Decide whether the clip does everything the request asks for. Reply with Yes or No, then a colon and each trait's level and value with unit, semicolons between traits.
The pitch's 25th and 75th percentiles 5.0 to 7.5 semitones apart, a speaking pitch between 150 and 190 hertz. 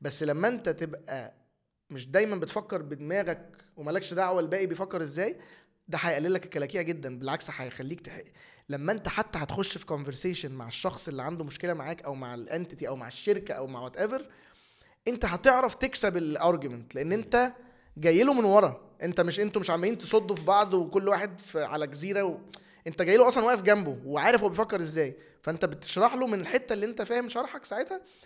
Yes: average, 5.3 semitones; medium, 185 Hz